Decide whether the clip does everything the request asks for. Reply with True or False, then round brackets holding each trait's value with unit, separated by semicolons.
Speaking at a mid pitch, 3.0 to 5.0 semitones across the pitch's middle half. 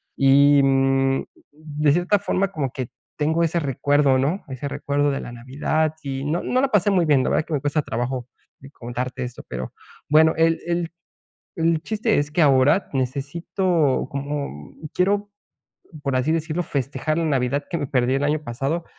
True (145 Hz; 3.5 semitones)